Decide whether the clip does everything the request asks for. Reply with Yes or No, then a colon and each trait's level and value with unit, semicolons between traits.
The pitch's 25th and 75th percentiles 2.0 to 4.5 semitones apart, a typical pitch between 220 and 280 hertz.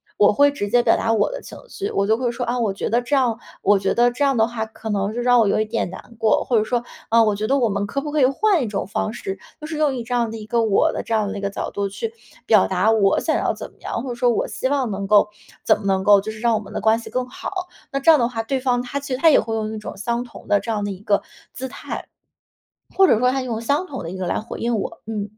Yes: average, 3.3 semitones; high, 230 Hz